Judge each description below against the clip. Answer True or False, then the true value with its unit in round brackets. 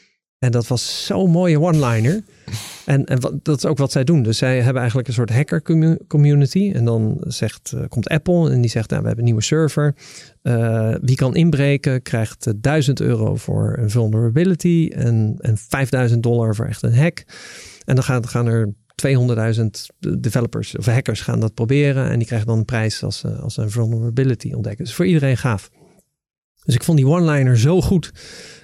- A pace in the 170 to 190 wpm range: True (185 wpm)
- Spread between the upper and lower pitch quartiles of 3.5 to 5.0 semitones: True (4.3 semitones)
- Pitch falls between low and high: False (130 Hz)